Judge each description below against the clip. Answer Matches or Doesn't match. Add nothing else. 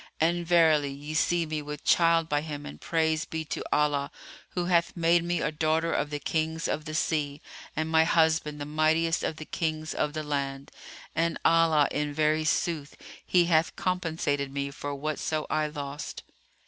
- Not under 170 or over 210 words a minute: Matches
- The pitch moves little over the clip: Matches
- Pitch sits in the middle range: Matches